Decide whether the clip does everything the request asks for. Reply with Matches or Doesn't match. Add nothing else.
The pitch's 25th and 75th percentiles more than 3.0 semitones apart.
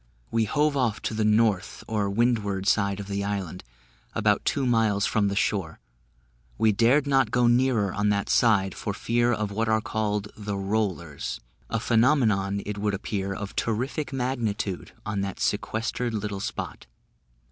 Doesn't match